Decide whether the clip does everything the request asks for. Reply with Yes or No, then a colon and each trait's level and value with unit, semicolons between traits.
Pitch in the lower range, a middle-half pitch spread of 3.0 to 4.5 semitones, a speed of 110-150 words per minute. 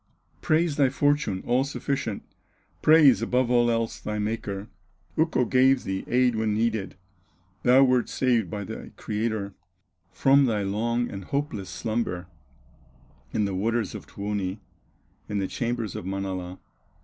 Yes: low, 115 Hz; average, 4.2 semitones; slow, 135 wpm